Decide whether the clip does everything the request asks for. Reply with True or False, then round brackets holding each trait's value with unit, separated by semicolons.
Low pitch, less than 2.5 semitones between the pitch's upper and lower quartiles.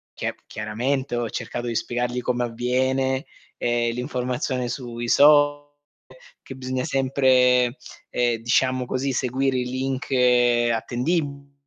True (125 Hz; 1.6 semitones)